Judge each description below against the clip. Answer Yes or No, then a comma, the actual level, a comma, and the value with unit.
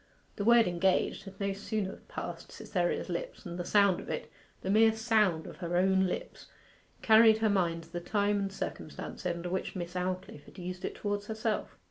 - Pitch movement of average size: Yes, average, 3.0 semitones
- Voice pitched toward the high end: Yes, high, 195 Hz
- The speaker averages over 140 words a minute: Yes, average, 190 wpm